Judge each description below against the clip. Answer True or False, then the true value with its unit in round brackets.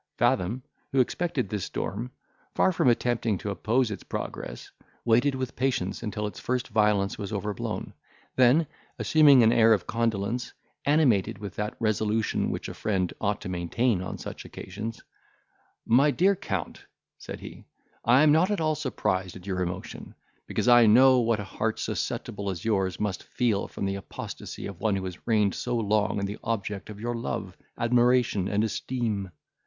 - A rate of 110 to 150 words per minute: False (170 wpm)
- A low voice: True (110 Hz)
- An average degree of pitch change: True (3.8 semitones)